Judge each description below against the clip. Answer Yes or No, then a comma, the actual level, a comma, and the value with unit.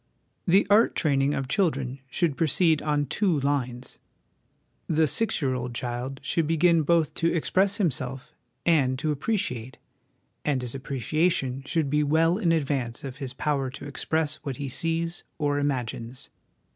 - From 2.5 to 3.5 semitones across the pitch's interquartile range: No, average, 3.9 semitones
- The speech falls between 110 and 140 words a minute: No, average, 155 wpm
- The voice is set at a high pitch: No, medium, 145 Hz